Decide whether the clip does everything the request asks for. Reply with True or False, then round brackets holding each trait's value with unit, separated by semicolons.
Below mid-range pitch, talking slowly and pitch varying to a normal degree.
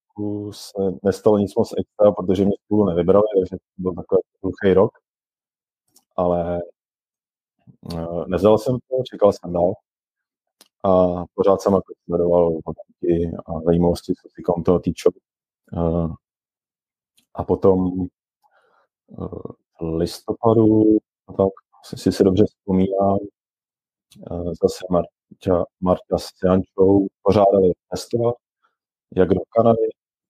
True (95 Hz; 105 wpm; 3.1 semitones)